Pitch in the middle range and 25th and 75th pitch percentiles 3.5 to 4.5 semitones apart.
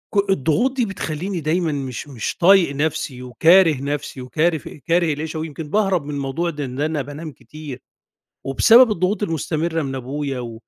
Yes: medium, 155 Hz; average, 3.8 semitones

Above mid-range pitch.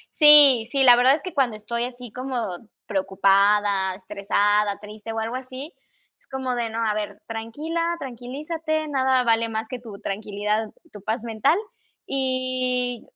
Yes: high, 240 Hz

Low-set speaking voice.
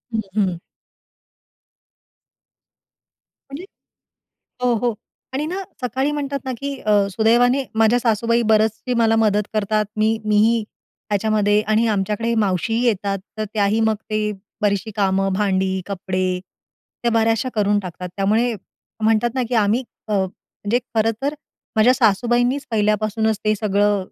No: high, 215 Hz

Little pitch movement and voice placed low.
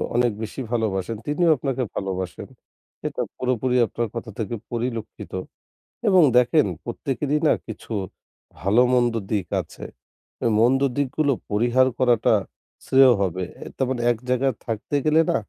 No: average, 3.0 semitones; low, 120 Hz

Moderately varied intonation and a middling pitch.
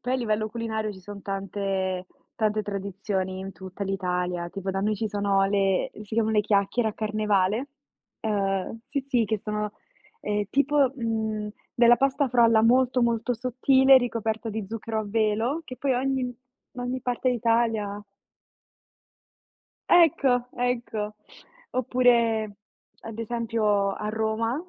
No: average, 3.2 semitones; high, 220 Hz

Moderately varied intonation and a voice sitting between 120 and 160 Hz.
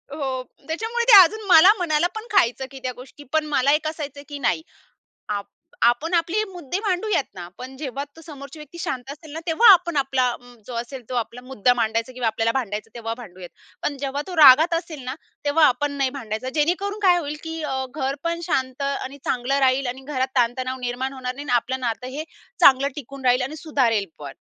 No: average, 4.0 semitones; very high, 275 Hz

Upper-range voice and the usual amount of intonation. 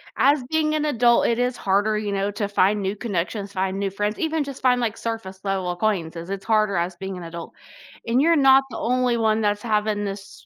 Yes: high, 210 Hz; average, 3.8 semitones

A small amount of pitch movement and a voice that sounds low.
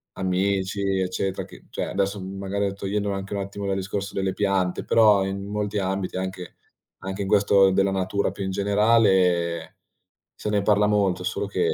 Yes: narrow, 1.1 semitones; low, 100 Hz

